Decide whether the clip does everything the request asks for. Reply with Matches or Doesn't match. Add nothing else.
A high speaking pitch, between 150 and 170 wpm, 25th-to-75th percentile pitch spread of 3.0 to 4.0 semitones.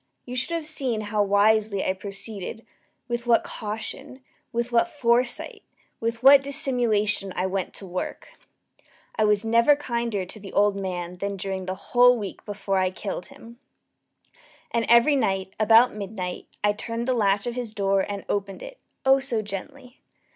Matches